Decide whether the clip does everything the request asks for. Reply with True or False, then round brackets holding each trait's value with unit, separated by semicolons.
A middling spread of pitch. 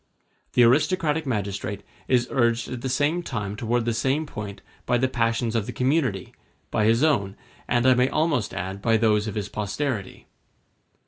True (3.8 semitones)